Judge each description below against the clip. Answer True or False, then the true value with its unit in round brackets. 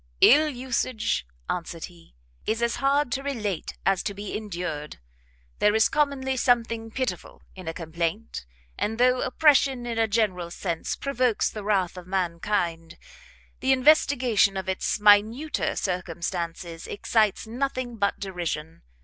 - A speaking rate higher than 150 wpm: False (135 wpm)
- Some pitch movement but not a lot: False (6.0 semitones)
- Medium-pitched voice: False (210 Hz)